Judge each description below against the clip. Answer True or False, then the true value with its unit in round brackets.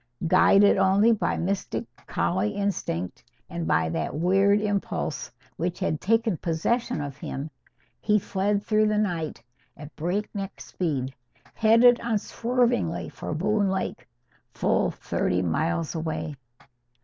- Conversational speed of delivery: False (120 wpm)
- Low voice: False (190 Hz)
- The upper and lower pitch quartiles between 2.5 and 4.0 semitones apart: False (5.3 semitones)